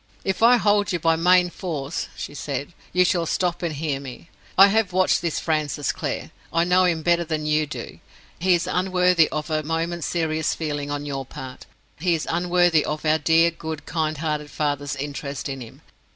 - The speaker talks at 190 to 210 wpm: Yes, average, 195 wpm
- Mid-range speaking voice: Yes, medium, 160 Hz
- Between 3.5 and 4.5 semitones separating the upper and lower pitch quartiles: No, average, 3.0 semitones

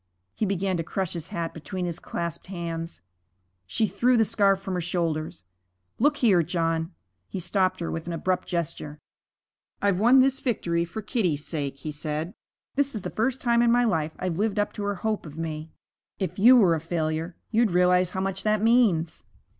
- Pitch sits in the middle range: Yes, medium, 180 Hz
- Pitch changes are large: No, average, 4.5 semitones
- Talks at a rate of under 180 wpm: No, average, 195 wpm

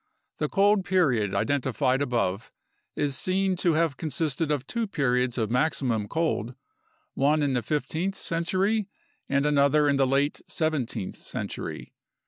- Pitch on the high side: No, medium, 145 Hz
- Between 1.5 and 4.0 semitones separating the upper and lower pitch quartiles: No, average, 4.5 semitones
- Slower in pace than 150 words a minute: Yes, slow, 135 wpm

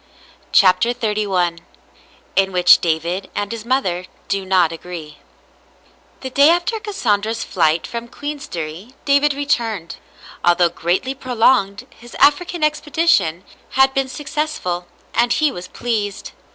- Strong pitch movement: Yes, wide, 7.3 semitones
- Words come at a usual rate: No, slow, 120 wpm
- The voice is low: No, high, 220 Hz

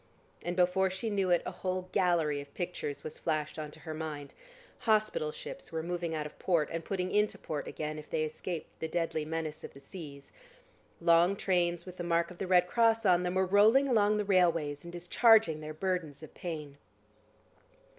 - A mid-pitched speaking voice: Yes, medium, 175 Hz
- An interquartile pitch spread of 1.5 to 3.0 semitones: No, average, 3.4 semitones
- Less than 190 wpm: No, average, 195 wpm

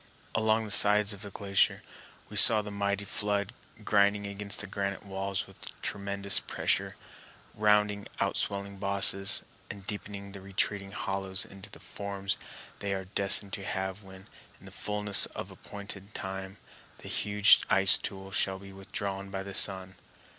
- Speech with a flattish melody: Yes, narrow, 0.9 semitones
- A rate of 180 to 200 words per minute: No, average, 155 wpm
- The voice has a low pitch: Yes, low, 100 Hz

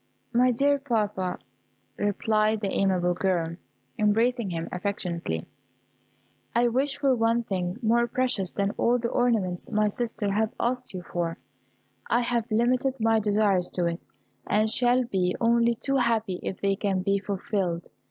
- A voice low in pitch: No, high, 215 Hz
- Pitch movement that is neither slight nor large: Yes, average, 4.0 semitones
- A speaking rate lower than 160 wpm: Yes, average, 150 wpm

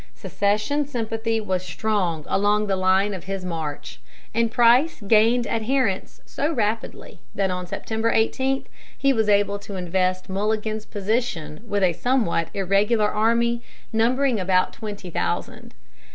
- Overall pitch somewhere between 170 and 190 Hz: No, high, 210 Hz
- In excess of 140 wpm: No, slow, 135 wpm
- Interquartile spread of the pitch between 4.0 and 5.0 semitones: No, average, 3.4 semitones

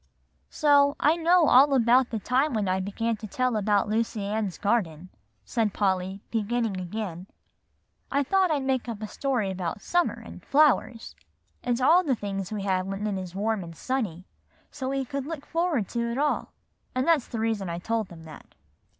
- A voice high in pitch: Yes, high, 225 Hz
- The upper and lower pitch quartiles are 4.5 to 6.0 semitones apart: Yes, wide, 5.4 semitones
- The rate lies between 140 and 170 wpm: No, average, 185 wpm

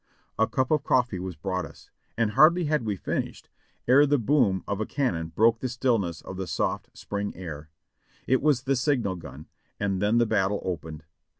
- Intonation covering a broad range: Yes, wide, 5.8 semitones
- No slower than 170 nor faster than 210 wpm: Yes, average, 195 wpm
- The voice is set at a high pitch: No, low, 110 Hz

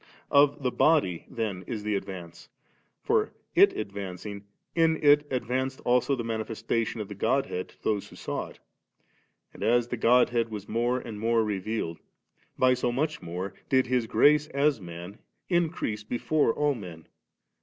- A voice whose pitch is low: Yes, low, 115 Hz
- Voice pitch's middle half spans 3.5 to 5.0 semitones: Yes, average, 4.5 semitones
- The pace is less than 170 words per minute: Yes, average, 160 wpm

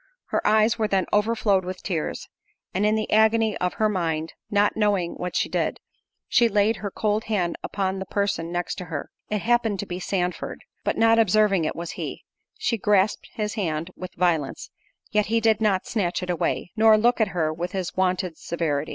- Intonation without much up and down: No, average, 3.3 semitones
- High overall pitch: Yes, high, 195 Hz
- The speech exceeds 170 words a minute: Yes, average, 185 wpm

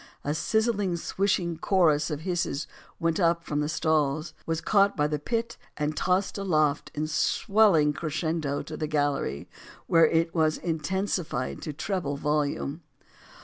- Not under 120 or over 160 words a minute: Yes, average, 145 wpm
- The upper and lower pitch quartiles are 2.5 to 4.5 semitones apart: Yes, average, 3.5 semitones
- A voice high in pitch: No, medium, 160 Hz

